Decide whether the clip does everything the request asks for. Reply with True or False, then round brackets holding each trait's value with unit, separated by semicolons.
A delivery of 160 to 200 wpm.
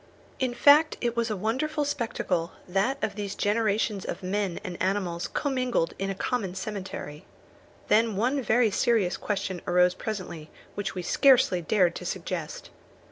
False (150 wpm)